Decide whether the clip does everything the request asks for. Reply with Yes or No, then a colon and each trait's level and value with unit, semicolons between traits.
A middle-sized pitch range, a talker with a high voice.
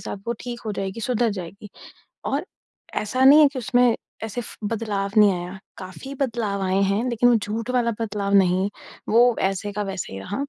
Yes: average, 3.5 semitones; high, 210 Hz